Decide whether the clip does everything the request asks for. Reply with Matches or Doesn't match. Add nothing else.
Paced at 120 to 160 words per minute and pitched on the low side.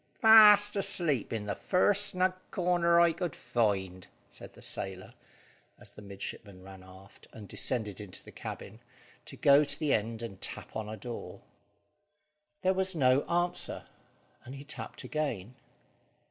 Matches